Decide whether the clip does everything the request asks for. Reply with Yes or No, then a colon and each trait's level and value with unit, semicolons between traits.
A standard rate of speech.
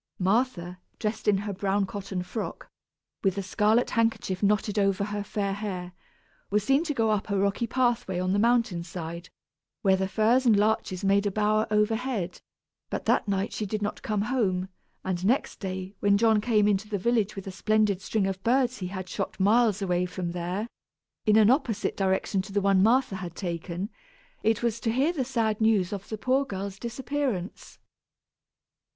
Yes: average, 185 wpm